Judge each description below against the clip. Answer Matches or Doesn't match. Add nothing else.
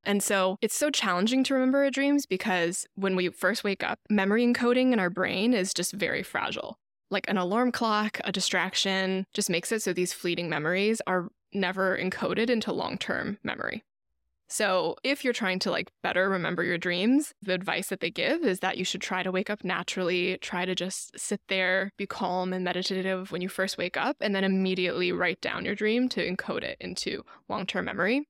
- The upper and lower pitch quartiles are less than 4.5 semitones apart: Matches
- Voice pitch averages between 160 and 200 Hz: Matches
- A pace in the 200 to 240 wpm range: Matches